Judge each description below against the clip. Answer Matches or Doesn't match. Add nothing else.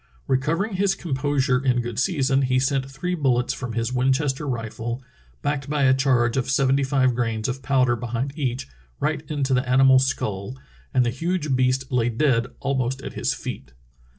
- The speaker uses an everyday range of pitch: Doesn't match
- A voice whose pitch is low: Matches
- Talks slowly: Doesn't match